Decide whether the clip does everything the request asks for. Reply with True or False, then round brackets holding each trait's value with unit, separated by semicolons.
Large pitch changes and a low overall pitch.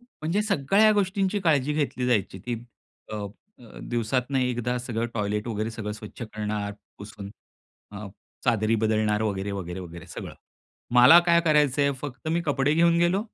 True (6.8 semitones; 120 Hz)